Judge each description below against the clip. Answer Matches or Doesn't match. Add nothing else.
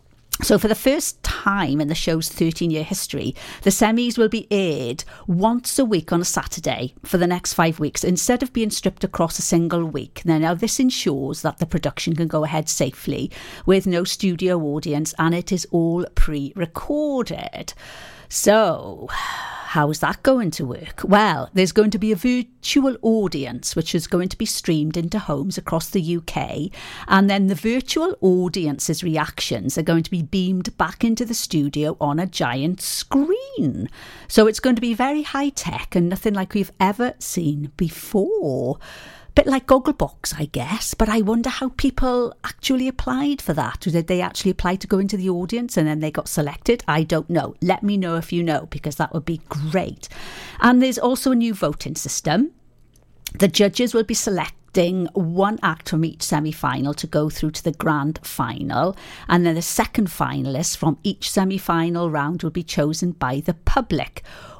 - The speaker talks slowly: Doesn't match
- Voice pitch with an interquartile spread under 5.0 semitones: Doesn't match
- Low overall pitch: Doesn't match